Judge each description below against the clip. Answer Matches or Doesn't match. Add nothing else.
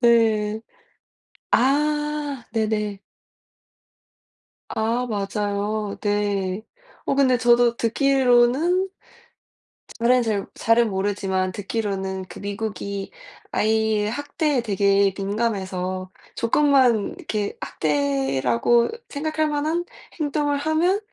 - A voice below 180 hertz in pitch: Doesn't match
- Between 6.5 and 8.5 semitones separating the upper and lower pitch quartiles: Doesn't match